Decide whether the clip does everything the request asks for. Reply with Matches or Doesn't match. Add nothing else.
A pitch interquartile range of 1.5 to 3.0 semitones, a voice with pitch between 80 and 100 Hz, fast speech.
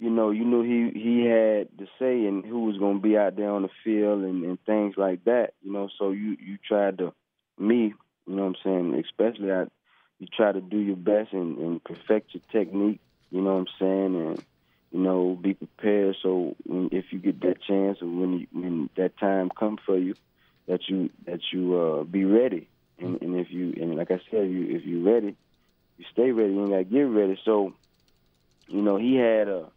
Matches